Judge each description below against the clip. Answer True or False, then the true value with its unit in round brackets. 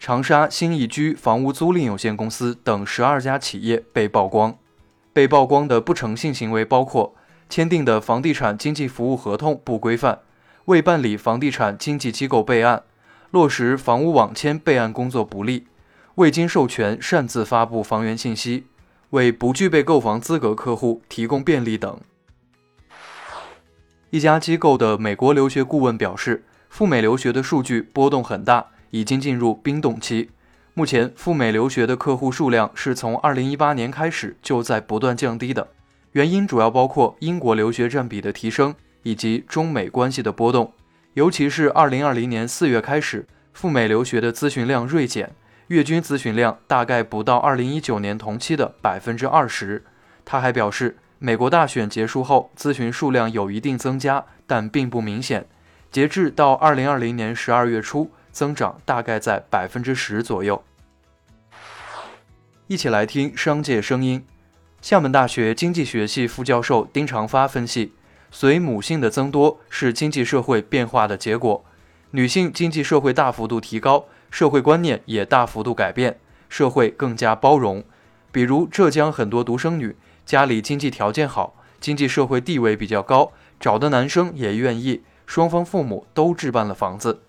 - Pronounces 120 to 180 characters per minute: False (265 characters per minute)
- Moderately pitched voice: False (125 Hz)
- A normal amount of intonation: True (4.4 semitones)